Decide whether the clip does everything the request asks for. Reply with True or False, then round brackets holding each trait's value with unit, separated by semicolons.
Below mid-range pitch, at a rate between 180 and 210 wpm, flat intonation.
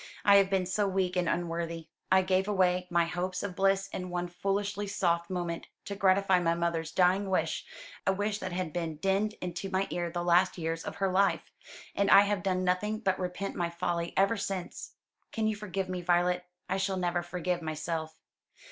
False (185 Hz; 195 wpm; 2.0 semitones)